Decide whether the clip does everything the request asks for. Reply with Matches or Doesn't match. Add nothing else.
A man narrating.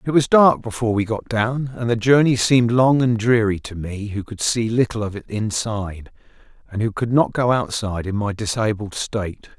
Matches